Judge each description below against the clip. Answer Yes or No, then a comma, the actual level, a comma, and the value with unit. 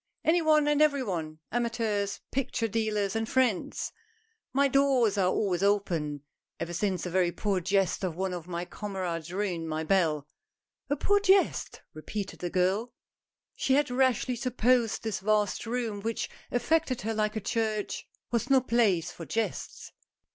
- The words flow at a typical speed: Yes, average, 160 wpm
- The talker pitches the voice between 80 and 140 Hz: No, high, 210 Hz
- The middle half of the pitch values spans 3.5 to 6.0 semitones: Yes, average, 5.2 semitones